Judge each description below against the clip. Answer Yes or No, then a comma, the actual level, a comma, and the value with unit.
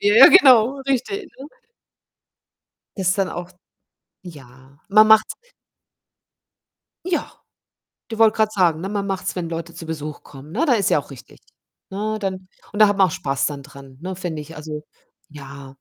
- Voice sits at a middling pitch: Yes, medium, 180 Hz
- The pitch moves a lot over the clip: Yes, wide, 6.3 semitones